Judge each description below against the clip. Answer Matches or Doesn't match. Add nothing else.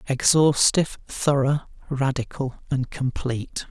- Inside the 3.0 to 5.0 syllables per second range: Matches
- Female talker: Doesn't match